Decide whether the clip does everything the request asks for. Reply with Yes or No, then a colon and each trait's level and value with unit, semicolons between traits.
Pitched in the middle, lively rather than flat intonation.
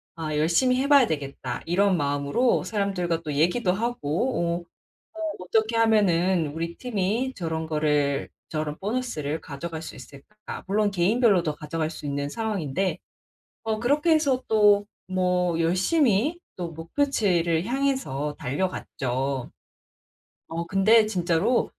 Yes: medium, 180 Hz; wide, 5.9 semitones